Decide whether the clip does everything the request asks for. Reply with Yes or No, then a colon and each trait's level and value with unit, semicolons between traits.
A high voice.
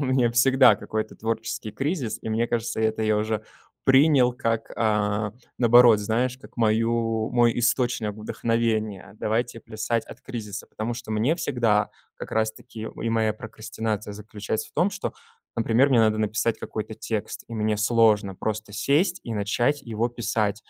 No: low, 115 Hz